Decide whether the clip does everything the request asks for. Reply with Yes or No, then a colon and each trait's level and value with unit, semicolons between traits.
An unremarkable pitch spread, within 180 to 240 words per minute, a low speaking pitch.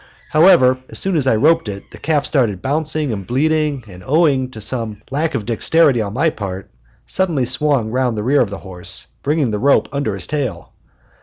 No: wide, 5.9 semitones; average, 200 wpm; low, 130 Hz